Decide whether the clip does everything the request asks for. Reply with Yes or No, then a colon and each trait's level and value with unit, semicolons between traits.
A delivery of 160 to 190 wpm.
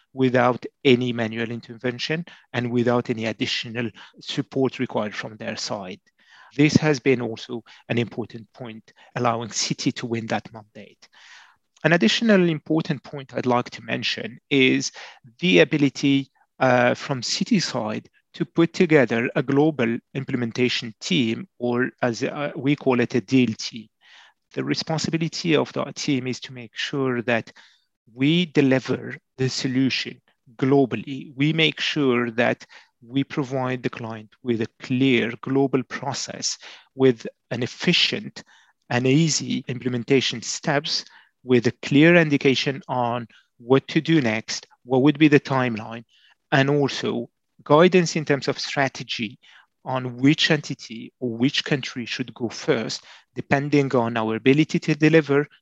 No: average, 140 wpm